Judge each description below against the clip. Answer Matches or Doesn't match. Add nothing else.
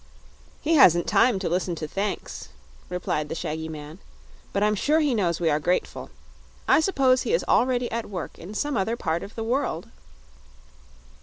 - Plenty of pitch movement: Matches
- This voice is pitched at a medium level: Doesn't match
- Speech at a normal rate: Matches